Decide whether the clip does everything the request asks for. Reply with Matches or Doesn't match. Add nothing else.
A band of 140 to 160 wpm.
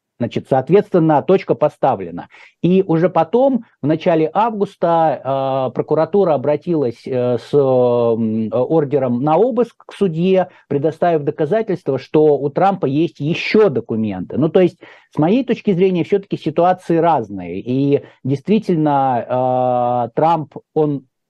Doesn't match